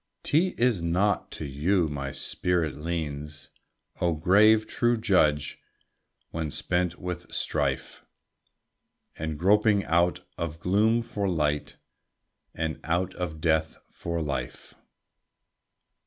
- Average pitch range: Yes, average, 4.2 semitones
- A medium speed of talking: No, slow, 110 wpm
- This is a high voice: No, very low, 85 Hz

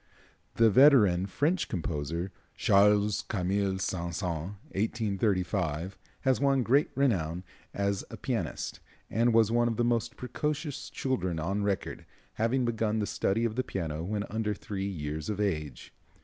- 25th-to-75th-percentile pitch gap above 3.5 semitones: Yes, average, 4.3 semitones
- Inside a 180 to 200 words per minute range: No, average, 150 wpm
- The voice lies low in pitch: Yes, low, 100 Hz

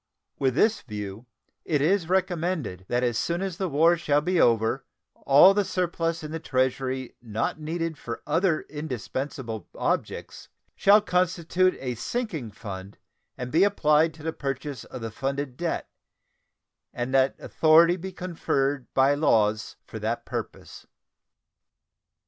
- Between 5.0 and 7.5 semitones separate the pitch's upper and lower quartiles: Yes, wide, 5.4 semitones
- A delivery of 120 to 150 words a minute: Yes, average, 140 wpm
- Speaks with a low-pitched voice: No, medium, 150 Hz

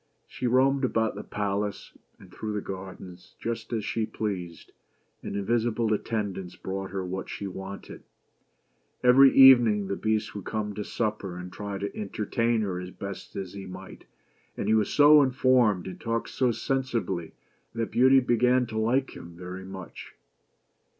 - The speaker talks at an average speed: Yes, average, 160 wpm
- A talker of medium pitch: No, low, 105 Hz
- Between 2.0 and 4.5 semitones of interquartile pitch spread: Yes, average, 3.7 semitones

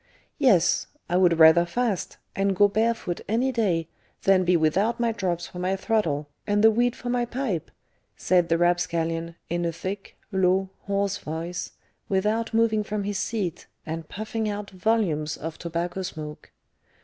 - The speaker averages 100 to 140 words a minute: No, average, 160 wpm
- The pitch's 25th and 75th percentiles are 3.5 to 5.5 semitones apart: Yes, average, 4.2 semitones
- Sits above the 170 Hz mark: Yes, high, 190 Hz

